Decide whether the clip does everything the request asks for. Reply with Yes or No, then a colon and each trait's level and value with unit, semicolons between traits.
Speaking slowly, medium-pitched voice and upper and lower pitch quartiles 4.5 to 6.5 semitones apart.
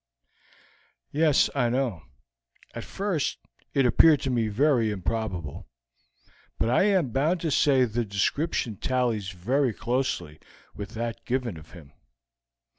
No: slow, 125 wpm; low, 120 Hz; average, 4.8 semitones